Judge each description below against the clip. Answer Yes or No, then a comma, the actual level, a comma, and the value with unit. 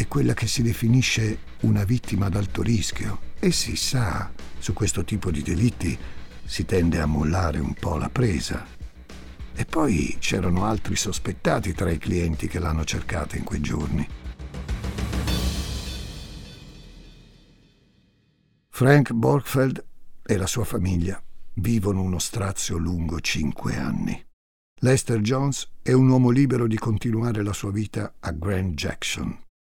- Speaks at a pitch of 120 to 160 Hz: No, low, 100 Hz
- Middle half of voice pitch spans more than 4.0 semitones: Yes, wide, 5.6 semitones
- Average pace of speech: Yes, average, 135 wpm